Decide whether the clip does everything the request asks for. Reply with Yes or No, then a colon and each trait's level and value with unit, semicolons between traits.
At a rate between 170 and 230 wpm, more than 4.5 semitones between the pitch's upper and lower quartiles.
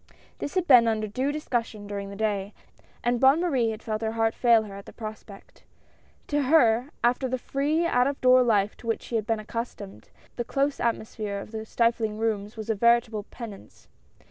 No: average, 195 wpm; average, 2.9 semitones